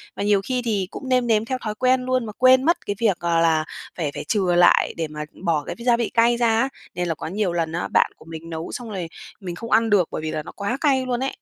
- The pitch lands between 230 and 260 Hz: No, high, 210 Hz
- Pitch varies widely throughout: Yes, wide, 6.4 semitones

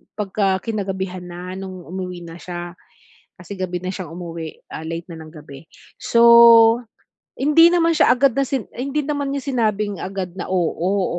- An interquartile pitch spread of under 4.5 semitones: No, average, 5.0 semitones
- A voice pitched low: No, high, 190 Hz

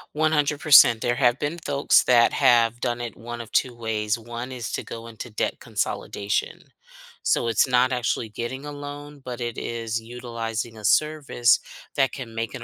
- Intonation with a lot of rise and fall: No, average, 2.7 semitones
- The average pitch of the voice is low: Yes, low, 120 Hz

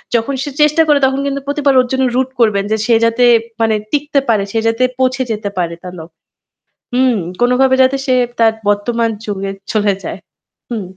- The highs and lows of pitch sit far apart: No, average, 3.6 semitones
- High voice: Yes, high, 240 Hz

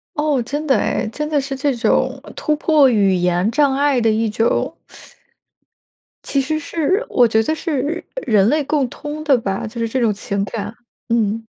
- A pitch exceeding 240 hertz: Yes, very high, 260 Hz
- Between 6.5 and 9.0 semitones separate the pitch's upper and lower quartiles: No, average, 5.1 semitones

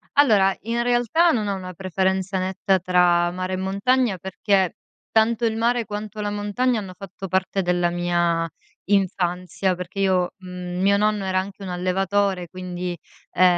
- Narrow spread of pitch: Yes, narrow, 2.3 semitones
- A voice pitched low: No, high, 190 Hz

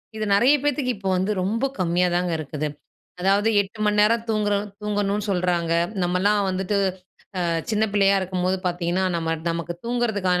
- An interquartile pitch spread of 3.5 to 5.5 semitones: No, average, 2.8 semitones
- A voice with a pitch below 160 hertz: No, high, 195 Hz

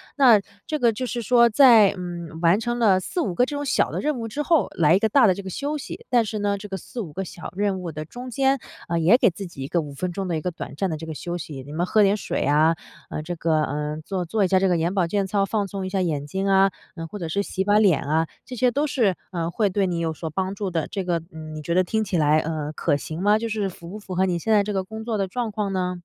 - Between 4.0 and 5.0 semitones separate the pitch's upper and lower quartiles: Yes, average, 4.4 semitones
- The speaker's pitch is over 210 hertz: No, high, 190 Hz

